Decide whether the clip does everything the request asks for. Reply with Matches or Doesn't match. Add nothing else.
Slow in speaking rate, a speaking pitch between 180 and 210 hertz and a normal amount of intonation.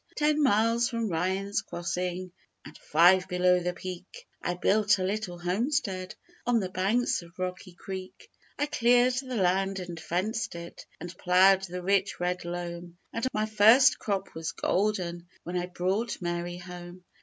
Doesn't match